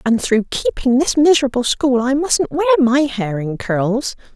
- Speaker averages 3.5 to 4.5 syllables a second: Yes, 4.3 syllables/s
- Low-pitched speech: No, very high, 260 Hz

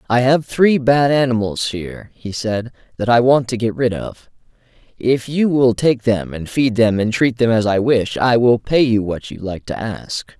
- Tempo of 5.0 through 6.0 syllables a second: No, 4.5 syllables/s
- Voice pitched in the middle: No, low, 120 Hz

